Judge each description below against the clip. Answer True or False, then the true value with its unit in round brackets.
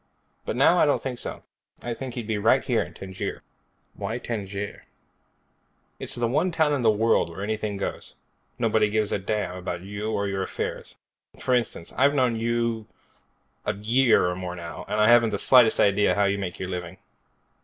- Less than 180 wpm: False (195 wpm)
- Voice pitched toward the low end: True (110 Hz)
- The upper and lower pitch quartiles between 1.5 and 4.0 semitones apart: True (3.4 semitones)